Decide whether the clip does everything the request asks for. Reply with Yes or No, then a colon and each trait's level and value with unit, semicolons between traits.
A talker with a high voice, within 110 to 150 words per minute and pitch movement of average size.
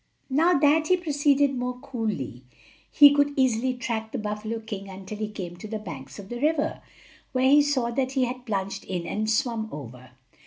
No: high, 235 Hz; average, 190 wpm; average, 5.0 semitones